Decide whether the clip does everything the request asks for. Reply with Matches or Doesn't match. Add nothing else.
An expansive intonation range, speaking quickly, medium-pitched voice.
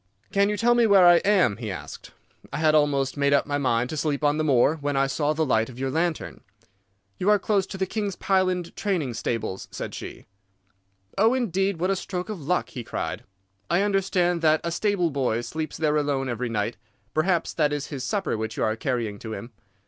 Matches